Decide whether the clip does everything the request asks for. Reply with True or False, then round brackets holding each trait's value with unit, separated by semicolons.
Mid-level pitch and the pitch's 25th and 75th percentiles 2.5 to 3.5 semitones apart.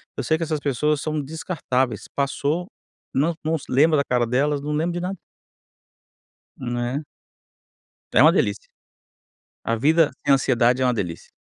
False (145 Hz; 4.0 semitones)